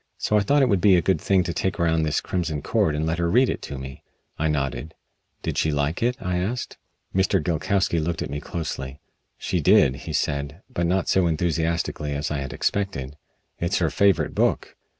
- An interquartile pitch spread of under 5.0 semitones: Yes, average, 4.2 semitones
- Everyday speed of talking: No, fast, 210 wpm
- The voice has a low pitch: Yes, very low, 85 Hz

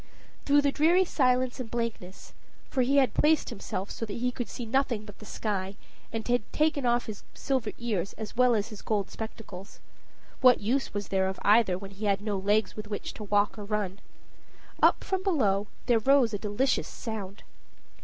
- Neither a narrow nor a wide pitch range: Yes, average, 3.8 semitones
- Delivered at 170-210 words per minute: Yes, average, 195 wpm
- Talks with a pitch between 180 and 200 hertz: No, high, 220 Hz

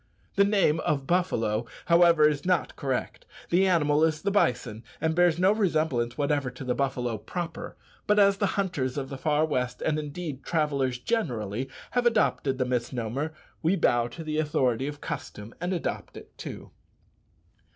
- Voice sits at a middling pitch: Yes, medium, 150 Hz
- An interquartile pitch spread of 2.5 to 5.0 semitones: No, wide, 5.6 semitones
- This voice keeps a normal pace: Yes, average, 165 wpm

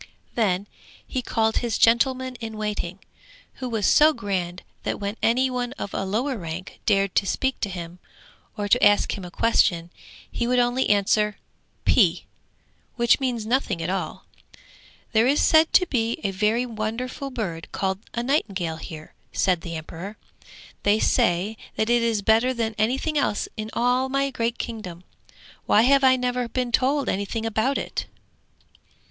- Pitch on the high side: Yes, high, 225 Hz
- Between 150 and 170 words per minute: Yes, average, 165 wpm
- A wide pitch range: No, average, 4.1 semitones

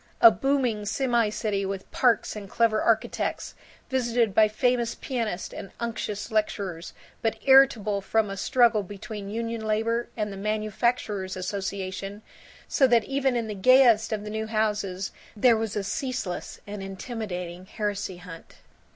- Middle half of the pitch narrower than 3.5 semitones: Yes, average, 2.8 semitones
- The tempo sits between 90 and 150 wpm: Yes, average, 145 wpm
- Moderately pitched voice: No, high, 215 Hz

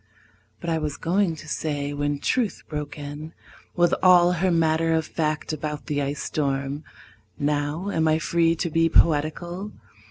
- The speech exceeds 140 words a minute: Yes, average, 160 wpm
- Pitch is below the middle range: No, medium, 155 Hz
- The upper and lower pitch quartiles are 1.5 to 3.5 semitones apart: Yes, narrow, 2.5 semitones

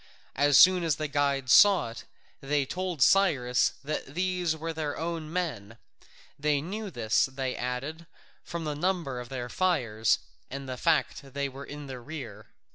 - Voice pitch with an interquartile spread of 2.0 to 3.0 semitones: No, average, 4.5 semitones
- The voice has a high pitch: No, medium, 145 Hz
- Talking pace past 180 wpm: No, average, 170 wpm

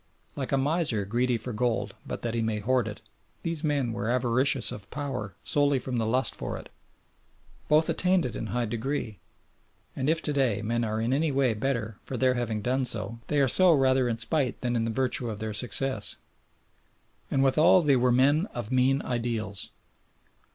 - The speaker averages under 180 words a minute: No, average, 190 wpm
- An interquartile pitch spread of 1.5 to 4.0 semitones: Yes, average, 3.3 semitones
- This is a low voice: Yes, low, 125 Hz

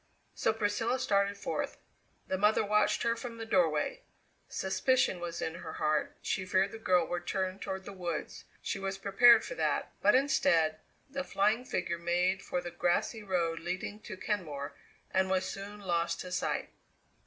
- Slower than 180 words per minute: Yes, average, 170 wpm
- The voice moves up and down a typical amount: Yes, average, 3.7 semitones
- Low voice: No, high, 190 Hz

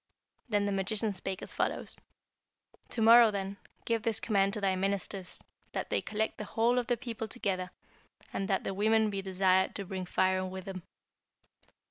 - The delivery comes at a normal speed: Yes, average, 175 wpm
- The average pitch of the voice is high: Yes, high, 200 Hz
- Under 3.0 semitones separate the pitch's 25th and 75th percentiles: Yes, narrow, 2.6 semitones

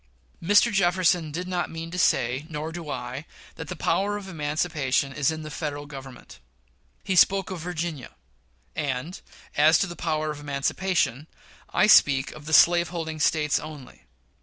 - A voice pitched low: No, medium, 155 Hz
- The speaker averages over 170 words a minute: No, average, 160 wpm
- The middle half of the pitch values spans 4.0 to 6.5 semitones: No, average, 3.3 semitones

